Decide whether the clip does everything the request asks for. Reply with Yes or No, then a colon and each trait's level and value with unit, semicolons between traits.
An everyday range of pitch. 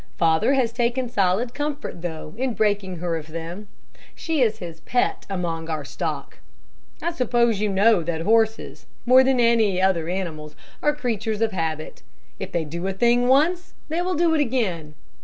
No: wide, 6.6 semitones